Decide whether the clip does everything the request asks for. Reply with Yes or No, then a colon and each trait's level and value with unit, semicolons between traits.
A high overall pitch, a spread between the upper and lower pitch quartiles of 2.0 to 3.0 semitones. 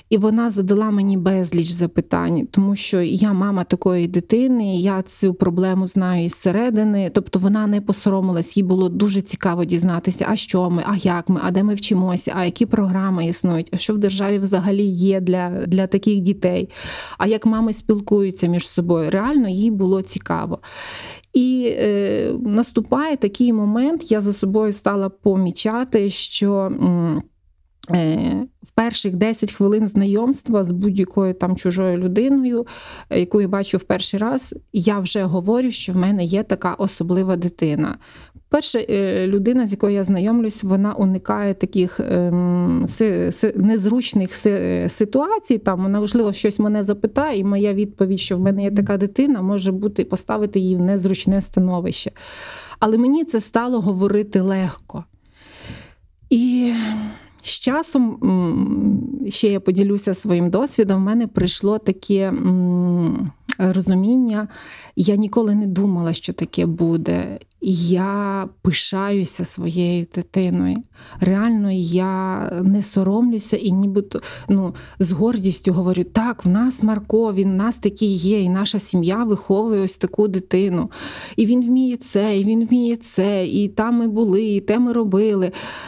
Yes: high, 200 Hz; narrow, 2.6 semitones